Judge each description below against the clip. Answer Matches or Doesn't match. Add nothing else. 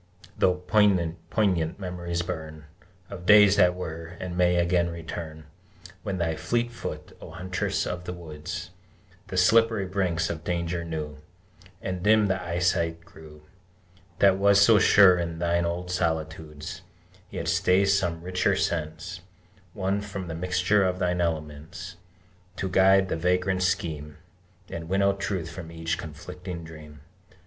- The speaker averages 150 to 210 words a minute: Doesn't match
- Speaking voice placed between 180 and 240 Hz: Doesn't match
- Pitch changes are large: Doesn't match